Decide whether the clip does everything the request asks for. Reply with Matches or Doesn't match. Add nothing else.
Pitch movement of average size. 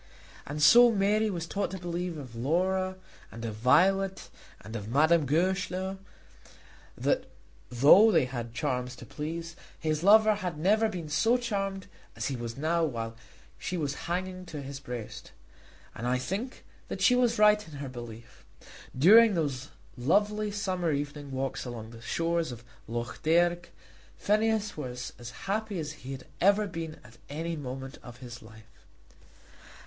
Doesn't match